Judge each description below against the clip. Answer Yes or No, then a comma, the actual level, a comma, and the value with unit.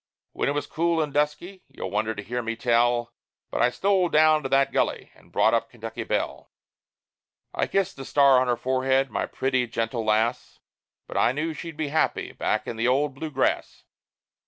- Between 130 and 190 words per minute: No, average, 200 wpm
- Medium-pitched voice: No, low, 130 Hz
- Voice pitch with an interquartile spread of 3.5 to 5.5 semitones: Yes, average, 4.3 semitones